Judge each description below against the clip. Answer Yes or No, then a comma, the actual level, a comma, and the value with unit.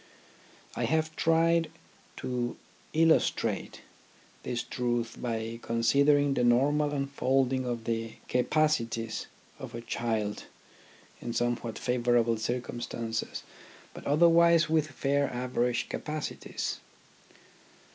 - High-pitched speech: No, low, 125 Hz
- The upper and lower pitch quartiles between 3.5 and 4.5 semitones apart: Yes, average, 4.2 semitones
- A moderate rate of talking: No, slow, 95 wpm